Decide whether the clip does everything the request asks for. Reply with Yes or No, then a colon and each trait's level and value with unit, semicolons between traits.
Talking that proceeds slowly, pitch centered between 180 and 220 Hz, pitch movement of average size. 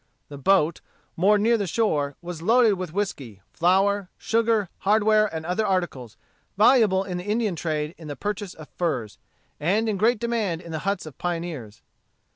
No: average, 170 wpm; medium, 185 Hz; average, 4.8 semitones